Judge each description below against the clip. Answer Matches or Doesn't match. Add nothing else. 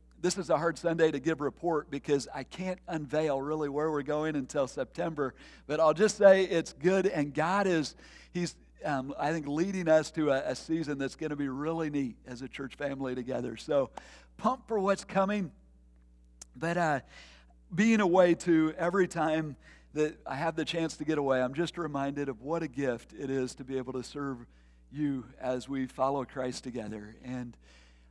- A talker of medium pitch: Matches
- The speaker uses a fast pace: Doesn't match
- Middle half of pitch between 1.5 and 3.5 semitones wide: Doesn't match